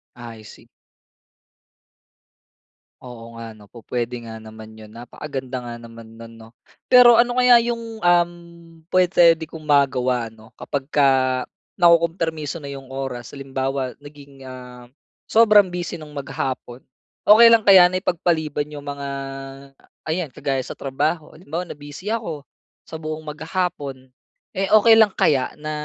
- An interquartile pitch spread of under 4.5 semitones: No, wide, 5.6 semitones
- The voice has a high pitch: No, medium, 145 Hz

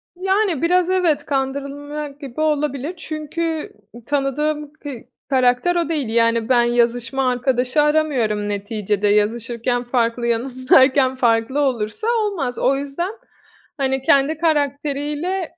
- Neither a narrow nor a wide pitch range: Yes, average, 4.0 semitones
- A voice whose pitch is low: No, very high, 275 Hz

